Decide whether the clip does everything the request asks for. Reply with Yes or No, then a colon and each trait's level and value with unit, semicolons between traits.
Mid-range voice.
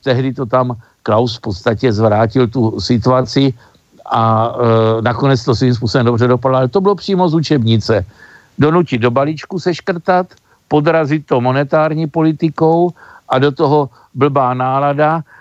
No: low, 130 Hz